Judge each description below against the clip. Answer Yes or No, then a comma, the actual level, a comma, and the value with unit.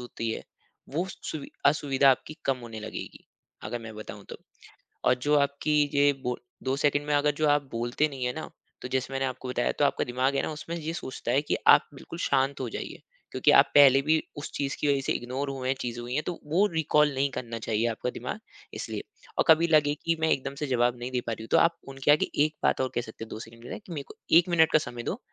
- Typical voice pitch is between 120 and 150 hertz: Yes, low, 135 Hz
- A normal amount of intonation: Yes, average, 3.3 semitones